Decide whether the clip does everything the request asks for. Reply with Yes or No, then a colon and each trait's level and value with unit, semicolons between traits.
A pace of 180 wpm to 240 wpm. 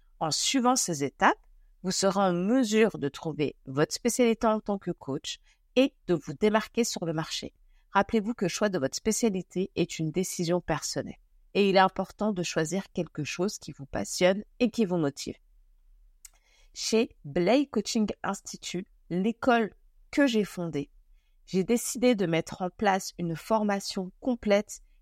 No: average, 160 wpm